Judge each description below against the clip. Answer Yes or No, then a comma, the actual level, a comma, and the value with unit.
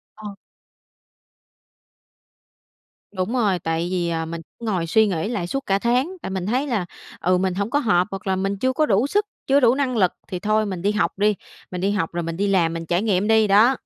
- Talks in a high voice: Yes, high, 200 Hz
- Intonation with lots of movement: No, average, 4.0 semitones